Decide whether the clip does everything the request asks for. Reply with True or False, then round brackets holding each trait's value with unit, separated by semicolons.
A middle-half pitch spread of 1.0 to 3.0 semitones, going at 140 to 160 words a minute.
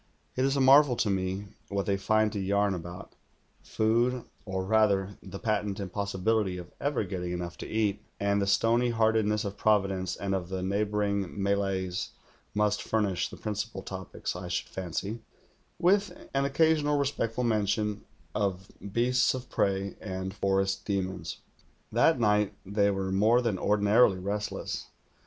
True (2.5 semitones; 150 wpm)